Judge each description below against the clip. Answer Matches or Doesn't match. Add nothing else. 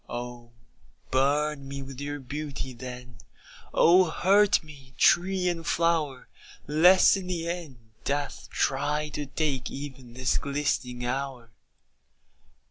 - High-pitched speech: Doesn't match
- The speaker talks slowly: Matches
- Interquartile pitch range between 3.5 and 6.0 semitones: Matches